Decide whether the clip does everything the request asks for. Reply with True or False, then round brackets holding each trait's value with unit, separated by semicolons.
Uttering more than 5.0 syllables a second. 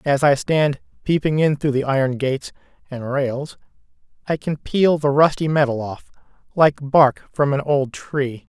False (4.4 syllables/s)